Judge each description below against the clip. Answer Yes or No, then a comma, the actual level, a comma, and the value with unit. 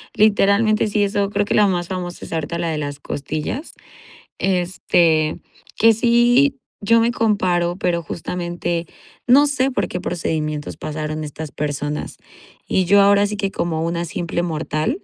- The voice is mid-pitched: Yes, medium, 180 Hz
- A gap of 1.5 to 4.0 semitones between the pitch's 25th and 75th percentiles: No, average, 4.4 semitones